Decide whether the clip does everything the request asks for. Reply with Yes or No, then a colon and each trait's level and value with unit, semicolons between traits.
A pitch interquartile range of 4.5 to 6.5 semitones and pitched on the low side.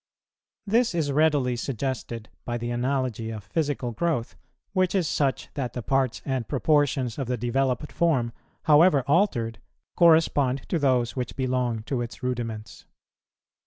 No: average, 3.7 semitones; low, 130 Hz